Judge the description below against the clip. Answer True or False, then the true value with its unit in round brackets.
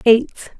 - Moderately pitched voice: False (230 Hz)